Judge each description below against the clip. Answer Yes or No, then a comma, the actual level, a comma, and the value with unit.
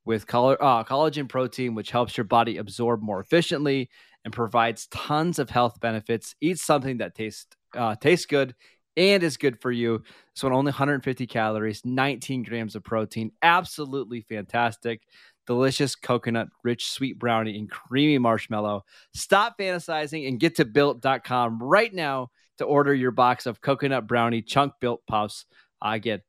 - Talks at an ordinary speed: Yes, average, 155 wpm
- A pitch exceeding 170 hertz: No, low, 125 Hz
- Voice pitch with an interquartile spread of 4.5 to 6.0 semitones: No, average, 3.6 semitones